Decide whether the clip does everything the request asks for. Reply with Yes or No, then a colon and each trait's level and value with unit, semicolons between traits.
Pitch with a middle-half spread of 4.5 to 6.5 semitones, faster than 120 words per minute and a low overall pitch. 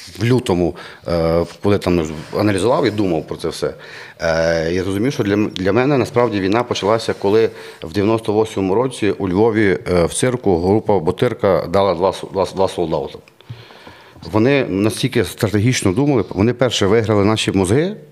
Yes: average, 5.0 semitones; average, 135 wpm; low, 105 Hz